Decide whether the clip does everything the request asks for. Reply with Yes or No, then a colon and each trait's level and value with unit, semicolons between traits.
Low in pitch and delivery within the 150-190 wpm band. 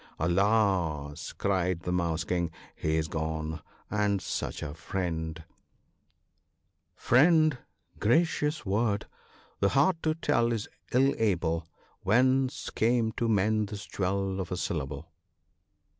No: very low, 95 Hz; average, 140 wpm